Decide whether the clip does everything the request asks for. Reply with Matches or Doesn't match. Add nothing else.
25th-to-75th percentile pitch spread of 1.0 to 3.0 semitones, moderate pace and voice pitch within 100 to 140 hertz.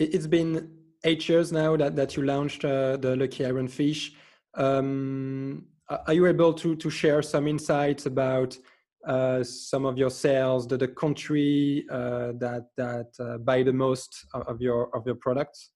Matches